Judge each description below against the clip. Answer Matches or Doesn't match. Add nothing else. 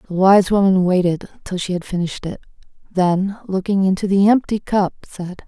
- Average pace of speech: Matches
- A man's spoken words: Doesn't match